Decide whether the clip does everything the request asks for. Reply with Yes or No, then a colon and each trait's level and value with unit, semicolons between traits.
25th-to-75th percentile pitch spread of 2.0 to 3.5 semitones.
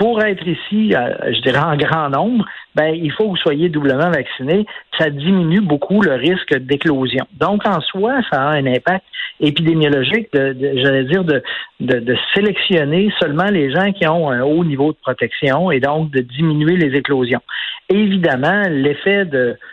No: average, 5.2 semitones